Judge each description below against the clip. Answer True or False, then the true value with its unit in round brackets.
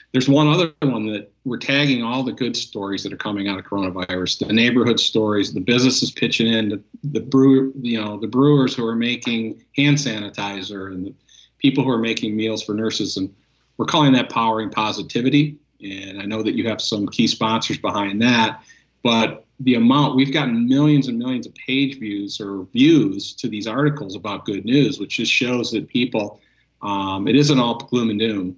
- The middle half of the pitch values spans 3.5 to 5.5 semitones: True (4.4 semitones)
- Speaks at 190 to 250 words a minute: True (195 wpm)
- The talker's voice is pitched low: True (115 Hz)